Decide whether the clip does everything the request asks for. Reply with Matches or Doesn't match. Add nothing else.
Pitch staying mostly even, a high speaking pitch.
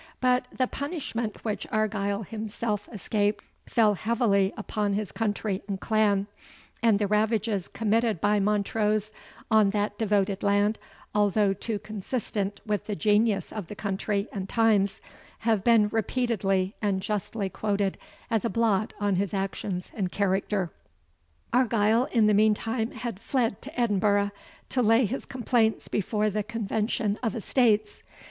Matches